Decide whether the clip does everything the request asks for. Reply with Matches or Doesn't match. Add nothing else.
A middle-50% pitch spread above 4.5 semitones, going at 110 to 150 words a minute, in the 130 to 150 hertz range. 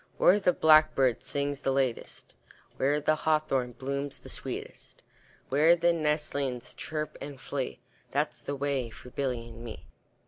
Doesn't match